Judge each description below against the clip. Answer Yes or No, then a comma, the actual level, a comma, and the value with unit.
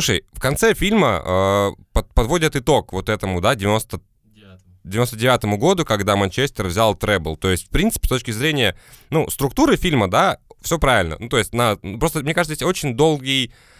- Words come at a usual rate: No, fast, 185 wpm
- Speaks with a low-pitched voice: Yes, low, 115 Hz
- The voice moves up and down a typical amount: No, wide, 7.1 semitones